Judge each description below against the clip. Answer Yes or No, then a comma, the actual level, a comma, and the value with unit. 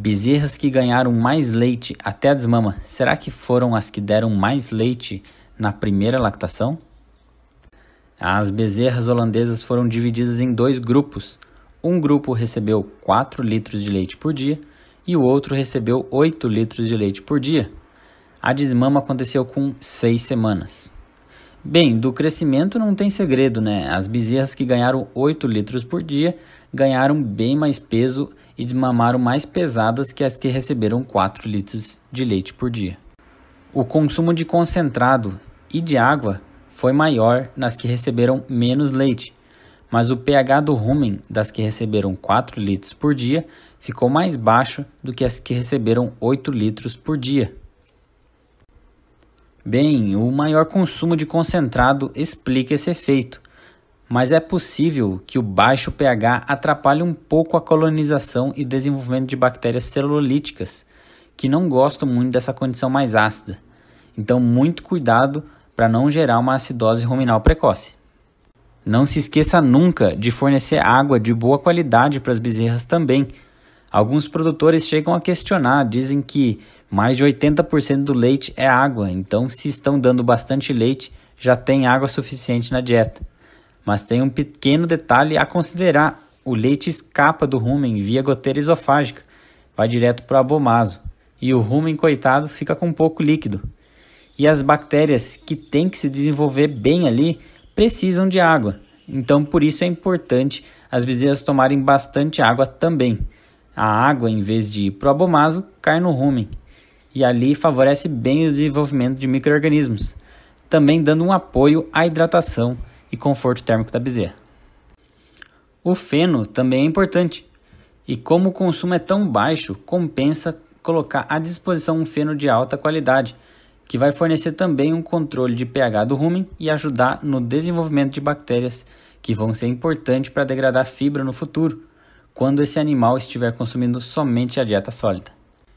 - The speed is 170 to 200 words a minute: No, average, 150 wpm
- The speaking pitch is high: No, low, 135 Hz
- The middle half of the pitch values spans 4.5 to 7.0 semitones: No, average, 4.1 semitones